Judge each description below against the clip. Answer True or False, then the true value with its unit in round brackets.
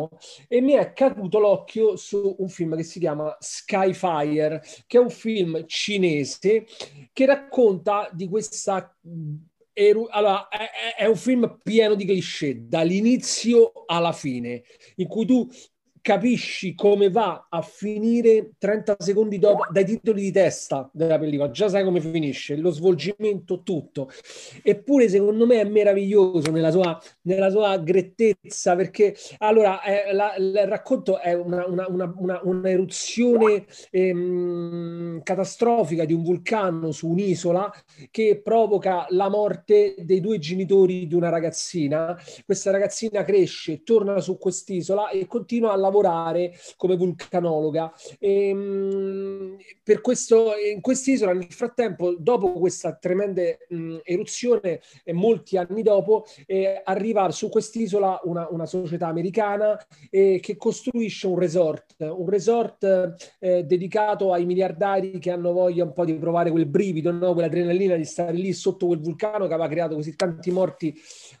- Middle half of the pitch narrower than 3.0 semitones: False (3.3 semitones)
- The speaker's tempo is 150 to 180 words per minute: False (140 wpm)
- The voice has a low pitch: False (190 Hz)